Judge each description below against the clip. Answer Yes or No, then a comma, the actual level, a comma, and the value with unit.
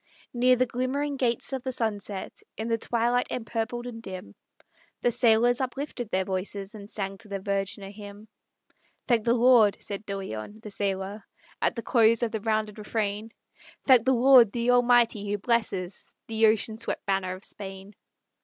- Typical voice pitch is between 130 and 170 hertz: No, high, 220 Hz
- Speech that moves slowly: No, average, 175 wpm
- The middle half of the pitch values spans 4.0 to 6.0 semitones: No, average, 3.1 semitones